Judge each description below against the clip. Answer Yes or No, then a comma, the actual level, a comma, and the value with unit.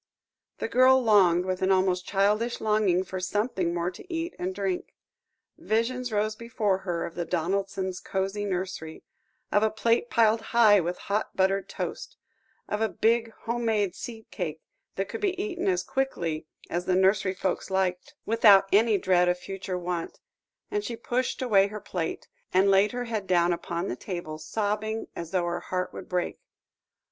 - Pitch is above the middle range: Yes, high, 195 Hz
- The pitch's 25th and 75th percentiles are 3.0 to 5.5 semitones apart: Yes, average, 3.7 semitones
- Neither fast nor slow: Yes, average, 175 wpm